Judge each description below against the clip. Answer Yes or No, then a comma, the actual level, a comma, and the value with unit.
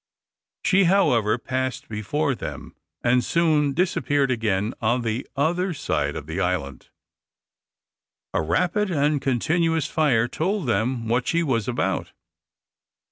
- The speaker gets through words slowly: Yes, slow, 125 wpm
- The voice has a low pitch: Yes, low, 130 Hz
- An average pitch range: No, wide, 6.1 semitones